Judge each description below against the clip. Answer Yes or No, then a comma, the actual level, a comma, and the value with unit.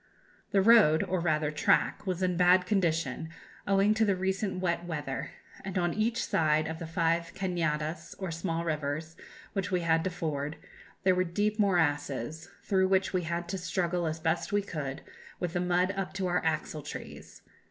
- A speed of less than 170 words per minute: No, average, 185 wpm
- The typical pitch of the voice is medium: Yes, medium, 175 Hz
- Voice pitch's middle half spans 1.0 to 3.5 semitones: Yes, average, 2.8 semitones